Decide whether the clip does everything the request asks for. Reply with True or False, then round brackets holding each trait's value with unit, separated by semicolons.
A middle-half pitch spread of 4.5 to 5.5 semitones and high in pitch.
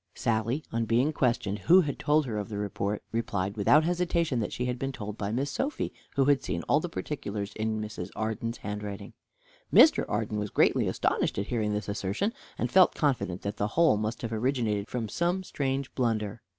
False (4.9 semitones; 115 Hz)